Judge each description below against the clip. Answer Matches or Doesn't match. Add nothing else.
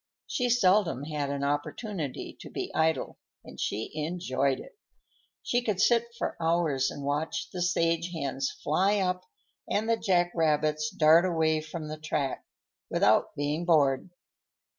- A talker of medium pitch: Matches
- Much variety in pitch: Doesn't match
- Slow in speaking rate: Doesn't match